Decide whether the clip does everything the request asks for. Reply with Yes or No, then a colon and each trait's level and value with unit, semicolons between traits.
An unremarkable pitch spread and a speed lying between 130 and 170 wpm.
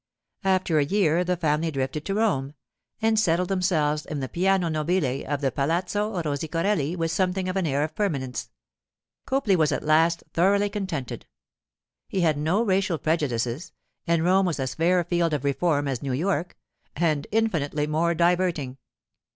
Yes: average, 4.1 semitones; average, 160 wpm